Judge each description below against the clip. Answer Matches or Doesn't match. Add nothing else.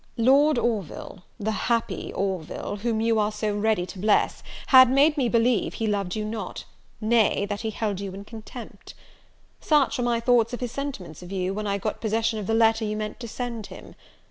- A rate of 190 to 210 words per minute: Matches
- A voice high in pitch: Matches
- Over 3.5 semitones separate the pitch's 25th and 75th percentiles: Doesn't match